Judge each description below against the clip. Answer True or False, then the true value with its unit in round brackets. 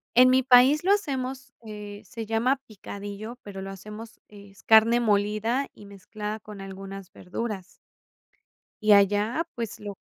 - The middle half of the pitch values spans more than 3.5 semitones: False (3.1 semitones)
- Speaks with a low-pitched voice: False (215 Hz)